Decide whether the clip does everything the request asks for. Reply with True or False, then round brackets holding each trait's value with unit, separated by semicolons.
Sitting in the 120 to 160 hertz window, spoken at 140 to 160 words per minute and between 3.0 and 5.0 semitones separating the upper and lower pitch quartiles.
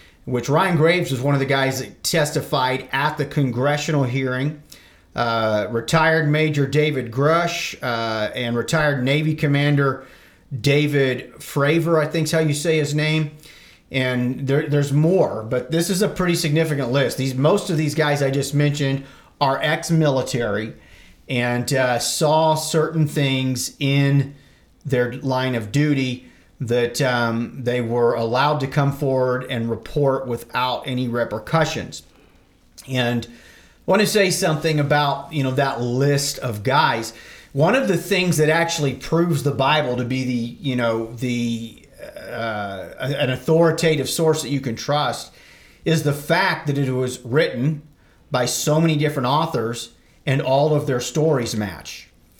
True (140 Hz; 150 wpm; 3.7 semitones)